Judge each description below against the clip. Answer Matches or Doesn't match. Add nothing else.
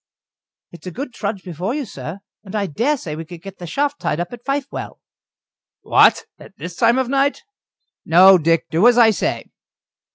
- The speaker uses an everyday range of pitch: Doesn't match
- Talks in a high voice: Matches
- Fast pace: Doesn't match